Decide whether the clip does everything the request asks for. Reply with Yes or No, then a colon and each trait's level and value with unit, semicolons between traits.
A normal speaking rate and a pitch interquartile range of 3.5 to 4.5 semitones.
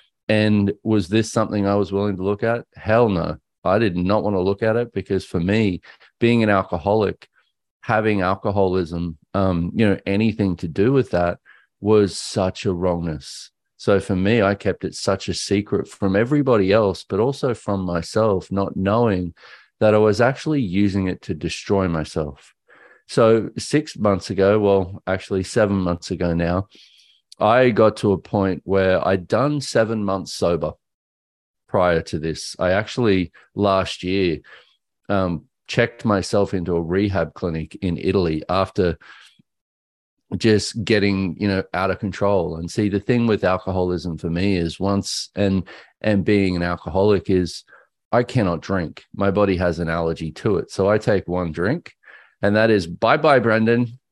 No: average, 165 wpm; average, 2.9 semitones